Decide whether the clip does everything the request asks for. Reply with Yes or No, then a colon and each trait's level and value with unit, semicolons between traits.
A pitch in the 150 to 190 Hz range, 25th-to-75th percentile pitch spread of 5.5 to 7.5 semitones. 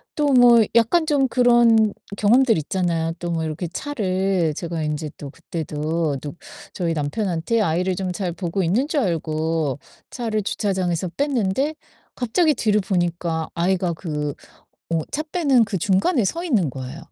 Yes: medium, 185 Hz; wide, 6.1 semitones